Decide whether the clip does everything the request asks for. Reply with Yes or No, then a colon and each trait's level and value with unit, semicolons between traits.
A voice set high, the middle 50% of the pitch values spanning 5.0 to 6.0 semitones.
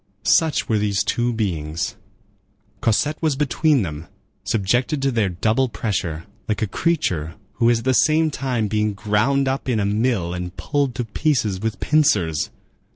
No: low, 110 Hz; wide, 5.4 semitones